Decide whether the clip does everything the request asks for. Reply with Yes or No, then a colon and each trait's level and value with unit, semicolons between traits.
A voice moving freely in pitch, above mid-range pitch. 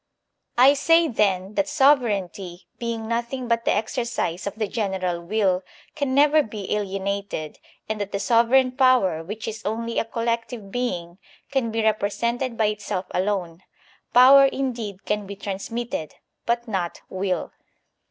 No: average, 3.8 semitones; high, 220 Hz